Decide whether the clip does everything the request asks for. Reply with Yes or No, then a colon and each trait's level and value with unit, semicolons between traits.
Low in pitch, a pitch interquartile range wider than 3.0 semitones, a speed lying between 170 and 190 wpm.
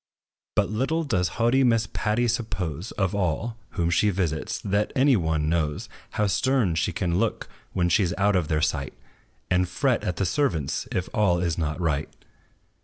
Yes: very low, 95 Hz; average, 5.2 semitones; average, 180 wpm